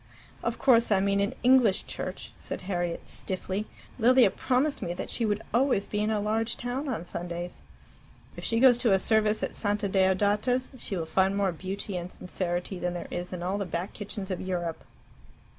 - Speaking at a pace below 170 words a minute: No, average, 195 wpm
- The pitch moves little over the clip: No, average, 3.6 semitones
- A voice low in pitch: No, high, 200 Hz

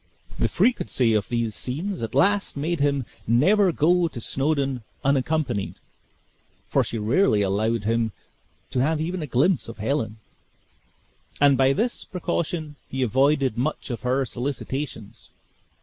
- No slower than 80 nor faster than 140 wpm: Yes, slow, 135 wpm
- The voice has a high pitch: No, low, 135 Hz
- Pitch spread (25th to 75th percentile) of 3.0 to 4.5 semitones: No, average, 5.1 semitones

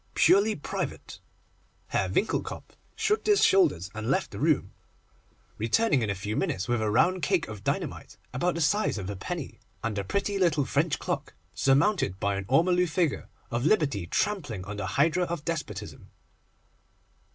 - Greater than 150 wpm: Yes, average, 165 wpm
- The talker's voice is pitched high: No, medium, 145 Hz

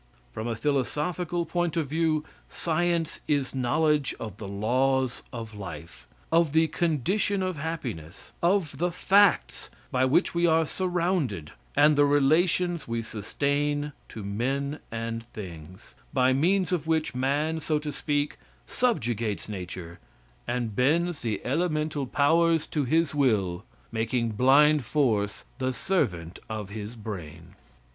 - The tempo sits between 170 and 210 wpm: No, slow, 135 wpm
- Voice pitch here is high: No, medium, 140 Hz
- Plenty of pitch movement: Yes, wide, 6.2 semitones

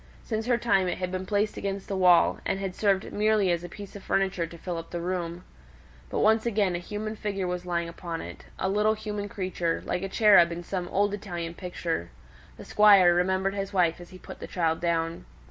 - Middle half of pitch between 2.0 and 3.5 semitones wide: Yes, average, 2.8 semitones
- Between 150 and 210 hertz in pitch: Yes, medium, 185 Hz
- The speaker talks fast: Yes, fast, 220 wpm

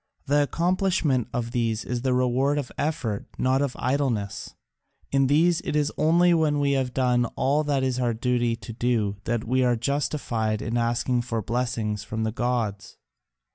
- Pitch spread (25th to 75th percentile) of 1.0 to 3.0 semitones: No, average, 3.4 semitones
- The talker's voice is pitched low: Yes, low, 125 Hz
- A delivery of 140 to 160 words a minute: No, average, 175 wpm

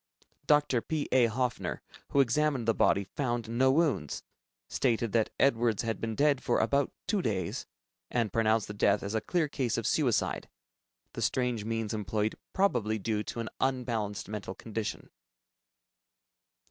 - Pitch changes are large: No, average, 3.6 semitones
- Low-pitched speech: Yes, low, 115 Hz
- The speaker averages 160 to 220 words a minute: No, average, 150 wpm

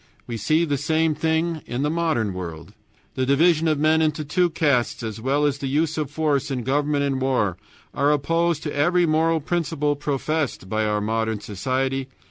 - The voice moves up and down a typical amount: Yes, average, 3.7 semitones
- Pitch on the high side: No, medium, 145 Hz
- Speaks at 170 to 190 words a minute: Yes, average, 185 wpm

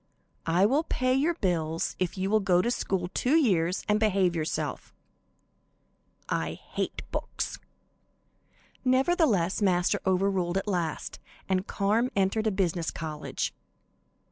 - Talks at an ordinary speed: No, slow, 125 wpm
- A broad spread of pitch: No, average, 3.9 semitones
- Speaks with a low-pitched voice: No, high, 195 Hz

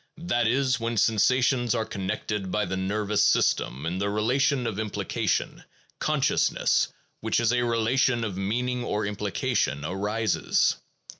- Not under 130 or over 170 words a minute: Yes, slow, 135 wpm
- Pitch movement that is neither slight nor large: Yes, average, 3.4 semitones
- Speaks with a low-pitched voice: Yes, low, 110 Hz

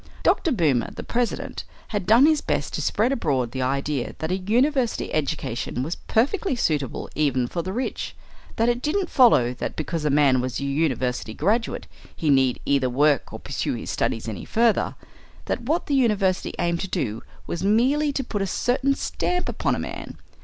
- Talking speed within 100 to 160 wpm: No, average, 185 wpm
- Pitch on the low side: No, medium, 175 Hz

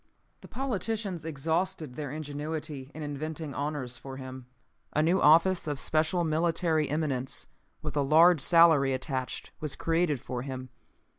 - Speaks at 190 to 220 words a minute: No, average, 140 wpm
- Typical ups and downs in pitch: Yes, average, 3.4 semitones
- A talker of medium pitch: Yes, medium, 155 Hz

